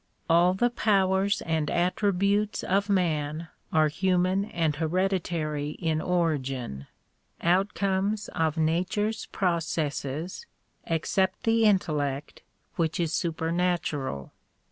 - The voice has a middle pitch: Yes, medium, 175 Hz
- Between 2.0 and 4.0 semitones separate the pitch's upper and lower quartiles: Yes, average, 3.6 semitones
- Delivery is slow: Yes, slow, 100 wpm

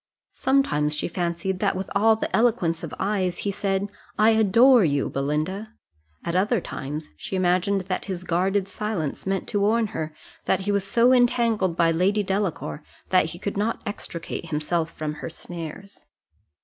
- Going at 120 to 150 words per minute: No, average, 165 wpm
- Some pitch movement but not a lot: Yes, average, 3.9 semitones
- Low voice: No, high, 190 Hz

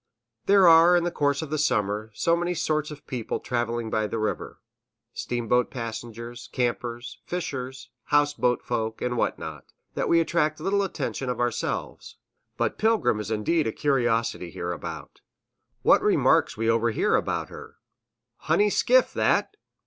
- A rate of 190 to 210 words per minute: No, average, 155 wpm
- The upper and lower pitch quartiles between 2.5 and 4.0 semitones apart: No, wide, 5.6 semitones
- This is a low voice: Yes, low, 125 Hz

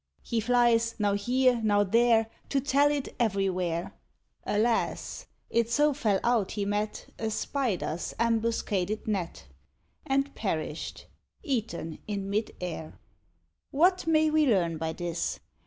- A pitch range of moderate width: Yes, average, 4.2 semitones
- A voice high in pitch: Yes, high, 220 Hz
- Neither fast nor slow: No, slow, 125 wpm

